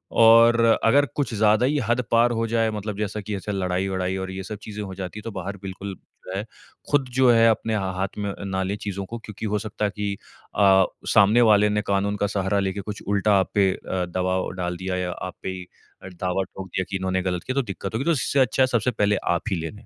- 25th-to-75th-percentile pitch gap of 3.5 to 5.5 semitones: No, average, 2.7 semitones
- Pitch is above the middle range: No, low, 100 Hz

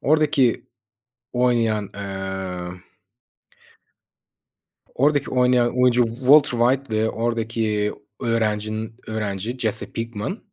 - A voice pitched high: No, low, 115 Hz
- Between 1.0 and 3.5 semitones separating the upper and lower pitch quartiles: Yes, average, 3.0 semitones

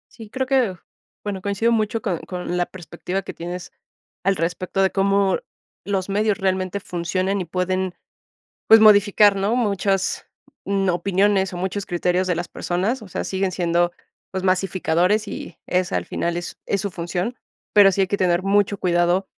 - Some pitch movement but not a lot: No, narrow, 2.1 semitones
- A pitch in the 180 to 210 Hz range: Yes, high, 190 Hz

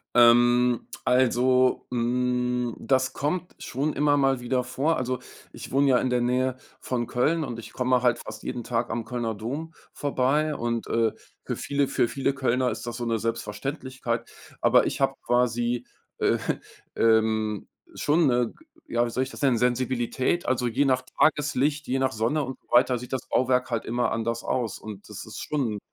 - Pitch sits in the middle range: No, low, 125 Hz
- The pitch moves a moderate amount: No, narrow, 1.9 semitones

